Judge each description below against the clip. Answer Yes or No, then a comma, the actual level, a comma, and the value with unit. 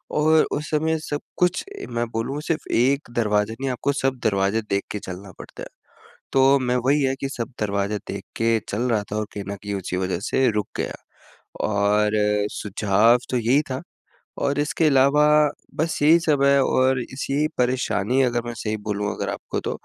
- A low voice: Yes, low, 125 Hz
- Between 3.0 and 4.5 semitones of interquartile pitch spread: No, average, 4.9 semitones